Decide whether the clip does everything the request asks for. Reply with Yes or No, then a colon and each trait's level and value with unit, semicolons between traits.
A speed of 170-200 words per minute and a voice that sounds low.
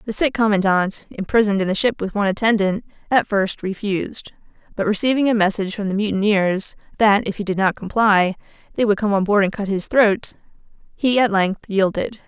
No: average, 190 wpm; high, 205 Hz